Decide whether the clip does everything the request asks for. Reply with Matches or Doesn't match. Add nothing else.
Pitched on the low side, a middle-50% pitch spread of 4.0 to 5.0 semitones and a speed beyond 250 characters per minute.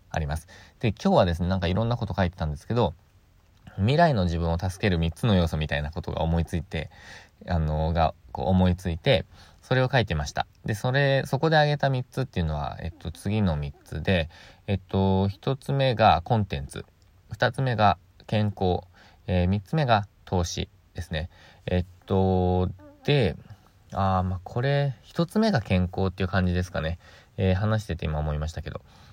Matches